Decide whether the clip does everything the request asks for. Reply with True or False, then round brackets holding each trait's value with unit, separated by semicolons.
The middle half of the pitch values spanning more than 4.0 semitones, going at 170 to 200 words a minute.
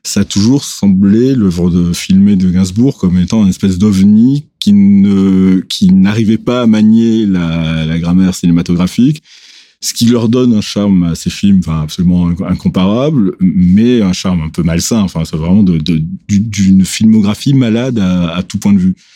True (5.2 semitones; 175 wpm)